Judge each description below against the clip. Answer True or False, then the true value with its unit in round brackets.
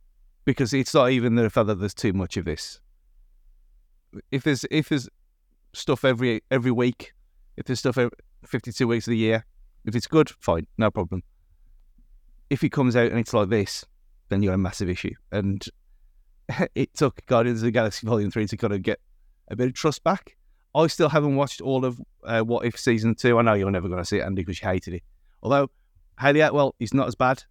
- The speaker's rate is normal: False (210 wpm)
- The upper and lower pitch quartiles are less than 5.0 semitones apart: False (5.5 semitones)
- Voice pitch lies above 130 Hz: False (115 Hz)